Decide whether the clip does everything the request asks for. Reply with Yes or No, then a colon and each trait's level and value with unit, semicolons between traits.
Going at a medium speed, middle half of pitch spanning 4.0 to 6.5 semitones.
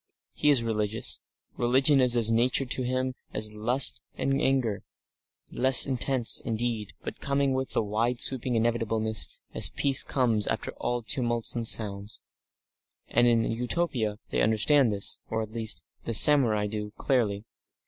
No: average, 150 wpm; average, 3.0 semitones